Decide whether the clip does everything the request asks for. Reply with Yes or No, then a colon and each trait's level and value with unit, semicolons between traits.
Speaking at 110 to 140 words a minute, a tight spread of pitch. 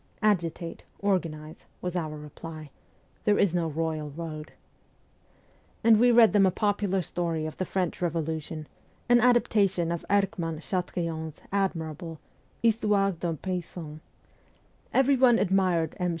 No: slow, 135 wpm; average, 3.9 semitones